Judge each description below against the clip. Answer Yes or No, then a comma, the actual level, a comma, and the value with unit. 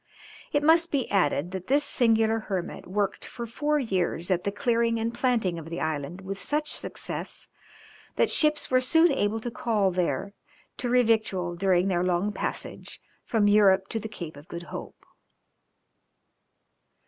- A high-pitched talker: Yes, high, 205 Hz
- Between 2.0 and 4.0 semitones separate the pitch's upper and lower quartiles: No, average, 4.9 semitones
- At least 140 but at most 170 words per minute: Yes, average, 160 wpm